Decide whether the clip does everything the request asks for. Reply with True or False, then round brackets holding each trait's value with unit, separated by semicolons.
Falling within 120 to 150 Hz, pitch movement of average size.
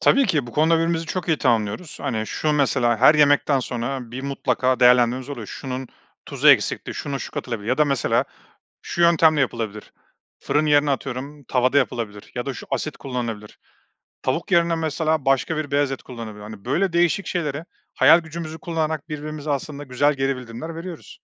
True (140 Hz; 4.0 semitones)